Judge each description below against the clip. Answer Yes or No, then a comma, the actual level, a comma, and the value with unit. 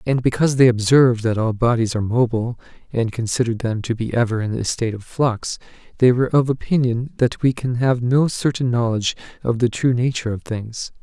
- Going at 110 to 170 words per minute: No, average, 200 wpm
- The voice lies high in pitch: No, low, 120 Hz